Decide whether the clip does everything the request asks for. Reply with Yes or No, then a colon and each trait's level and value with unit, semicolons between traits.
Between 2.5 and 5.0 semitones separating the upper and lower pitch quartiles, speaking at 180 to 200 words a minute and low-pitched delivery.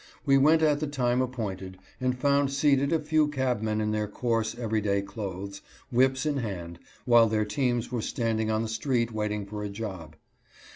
Yes: average, 4.0 semitones; average, 185 wpm; low, 115 Hz